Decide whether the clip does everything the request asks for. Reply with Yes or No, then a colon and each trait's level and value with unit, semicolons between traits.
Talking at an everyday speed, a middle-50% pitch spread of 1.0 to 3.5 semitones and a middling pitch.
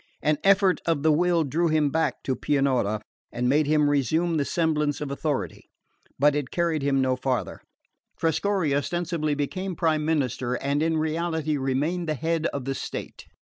Yes: average, 170 wpm; average, 2.9 semitones; medium, 150 Hz